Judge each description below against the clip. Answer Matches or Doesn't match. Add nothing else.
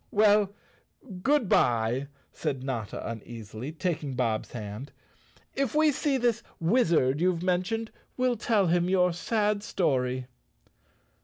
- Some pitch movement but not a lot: Doesn't match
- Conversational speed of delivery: Doesn't match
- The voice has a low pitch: Doesn't match